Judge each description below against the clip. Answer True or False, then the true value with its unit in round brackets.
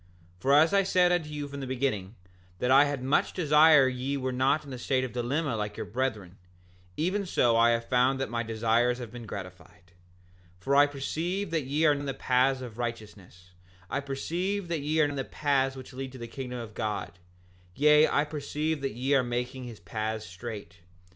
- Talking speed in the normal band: False (215 wpm)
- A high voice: False (130 Hz)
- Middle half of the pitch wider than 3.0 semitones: True (3.7 semitones)